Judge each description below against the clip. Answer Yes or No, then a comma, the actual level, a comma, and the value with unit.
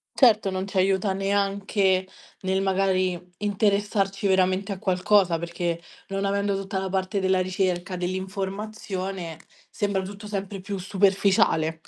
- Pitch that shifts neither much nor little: No, narrow, 1.2 semitones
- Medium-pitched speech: No, high, 195 Hz